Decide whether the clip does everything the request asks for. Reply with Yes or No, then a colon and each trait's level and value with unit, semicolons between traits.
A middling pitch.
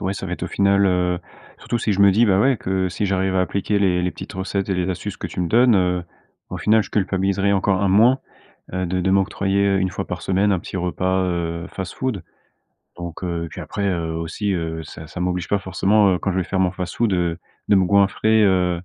No: very low, 95 Hz